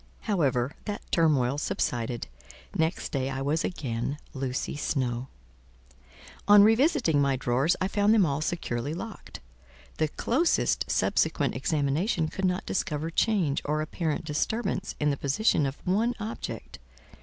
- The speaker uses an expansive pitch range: Yes, wide, 6.1 semitones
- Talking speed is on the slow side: Yes, slow, 130 wpm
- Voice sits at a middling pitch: Yes, medium, 155 Hz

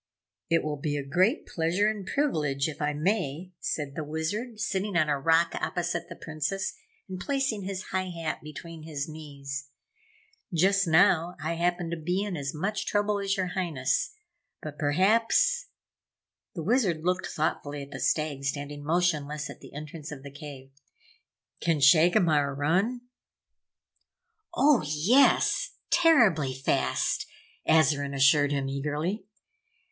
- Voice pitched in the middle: Yes, medium, 160 Hz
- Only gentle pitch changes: No, average, 4.6 semitones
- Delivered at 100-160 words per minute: Yes, average, 140 wpm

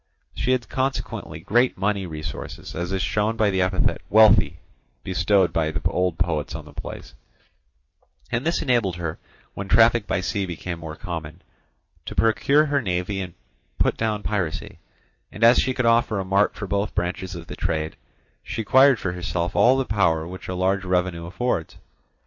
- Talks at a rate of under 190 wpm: Yes, average, 175 wpm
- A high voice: No, very low, 95 Hz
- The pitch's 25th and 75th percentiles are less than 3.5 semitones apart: No, average, 4.4 semitones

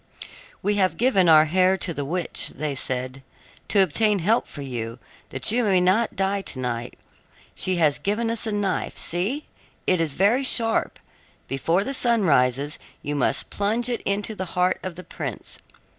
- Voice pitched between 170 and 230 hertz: Yes, medium, 185 Hz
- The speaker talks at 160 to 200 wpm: Yes, average, 175 wpm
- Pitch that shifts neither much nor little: No, wide, 6.1 semitones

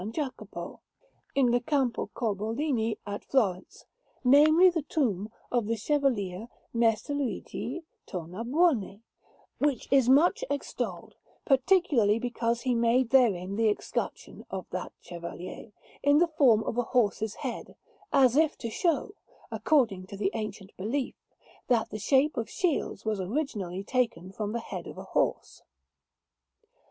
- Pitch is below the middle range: No, high, 235 Hz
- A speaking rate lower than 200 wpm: Yes, slow, 135 wpm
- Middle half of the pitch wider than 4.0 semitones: Yes, average, 5.0 semitones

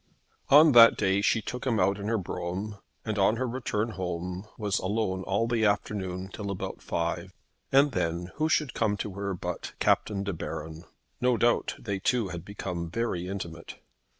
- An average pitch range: Yes, average, 3.9 semitones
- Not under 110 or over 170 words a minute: No, average, 180 wpm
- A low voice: Yes, low, 100 Hz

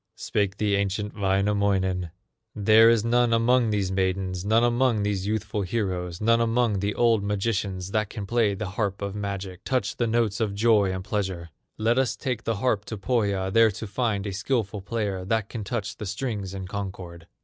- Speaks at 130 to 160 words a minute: No, average, 185 wpm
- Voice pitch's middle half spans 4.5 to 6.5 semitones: No, average, 2.8 semitones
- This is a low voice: Yes, low, 105 Hz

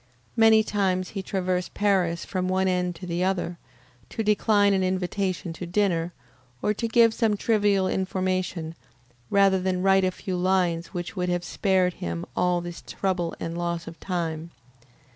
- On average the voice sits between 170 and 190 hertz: Yes, medium, 185 Hz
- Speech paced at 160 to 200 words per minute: Yes, average, 165 wpm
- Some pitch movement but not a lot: No, narrow, 2.1 semitones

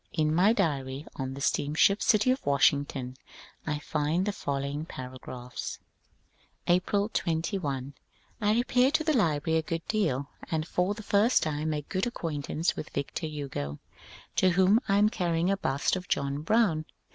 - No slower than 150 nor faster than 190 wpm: Yes, average, 160 wpm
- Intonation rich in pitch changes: Yes, wide, 5.7 semitones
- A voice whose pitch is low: No, medium, 160 Hz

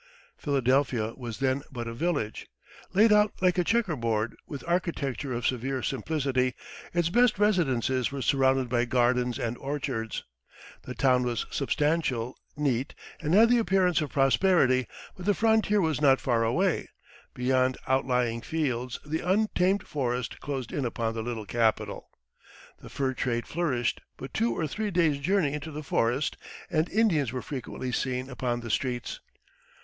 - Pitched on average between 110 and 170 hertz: Yes, low, 135 Hz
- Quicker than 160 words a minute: No, average, 155 wpm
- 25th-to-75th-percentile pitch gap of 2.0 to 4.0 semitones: No, average, 5.2 semitones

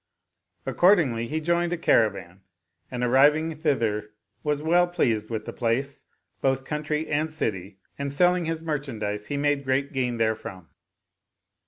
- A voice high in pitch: No, medium, 140 Hz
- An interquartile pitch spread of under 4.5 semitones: No, wide, 5.6 semitones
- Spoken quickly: No, average, 140 wpm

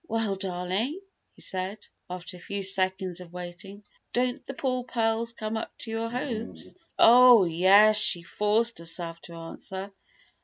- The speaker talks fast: No, average, 150 wpm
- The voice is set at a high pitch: Yes, high, 200 Hz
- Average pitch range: Yes, average, 4.0 semitones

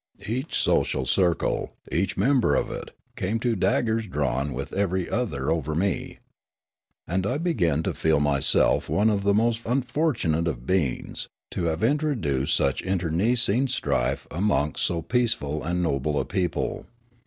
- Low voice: Yes, very low, 95 Hz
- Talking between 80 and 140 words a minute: No, average, 155 wpm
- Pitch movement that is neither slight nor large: No, wide, 7.0 semitones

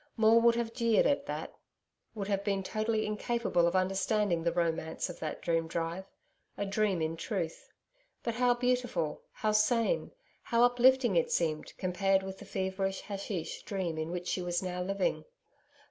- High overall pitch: Yes, high, 195 Hz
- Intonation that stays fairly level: No, average, 4.4 semitones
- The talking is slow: No, average, 165 wpm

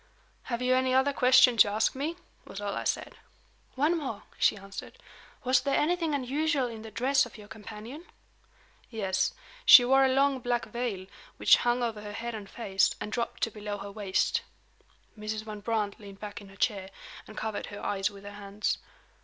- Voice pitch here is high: Yes, high, 225 Hz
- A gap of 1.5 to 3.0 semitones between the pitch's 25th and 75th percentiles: No, average, 4.0 semitones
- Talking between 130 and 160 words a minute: No, average, 190 wpm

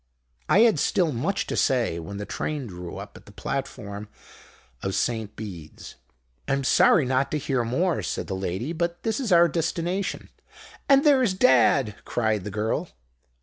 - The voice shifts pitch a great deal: Yes, wide, 8.5 semitones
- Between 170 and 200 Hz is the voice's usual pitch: No, low, 130 Hz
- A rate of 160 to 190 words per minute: Yes, average, 165 wpm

